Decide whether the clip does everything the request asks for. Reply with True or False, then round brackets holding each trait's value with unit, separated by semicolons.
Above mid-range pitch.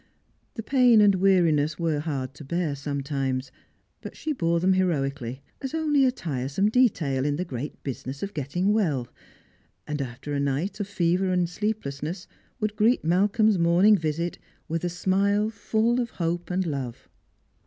False (170 Hz)